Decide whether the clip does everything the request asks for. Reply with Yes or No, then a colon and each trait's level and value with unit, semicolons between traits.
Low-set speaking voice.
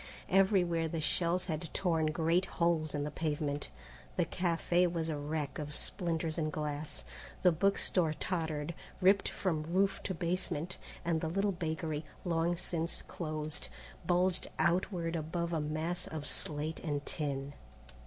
No: medium, 165 Hz